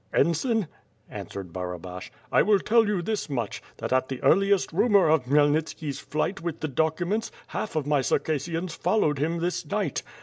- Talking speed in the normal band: Yes, average, 170 wpm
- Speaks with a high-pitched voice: No, medium, 160 Hz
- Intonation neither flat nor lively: No, wide, 5.8 semitones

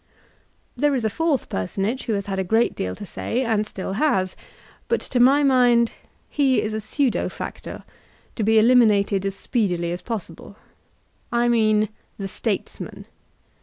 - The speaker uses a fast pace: No, average, 160 wpm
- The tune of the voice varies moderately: Yes, average, 3.9 semitones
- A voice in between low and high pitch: No, high, 220 Hz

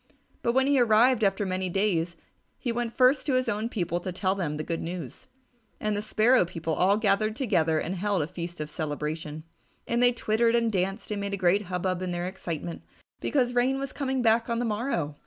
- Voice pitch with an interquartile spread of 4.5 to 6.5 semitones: Yes, average, 5.2 semitones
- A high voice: Yes, high, 200 Hz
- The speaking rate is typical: No, fast, 215 wpm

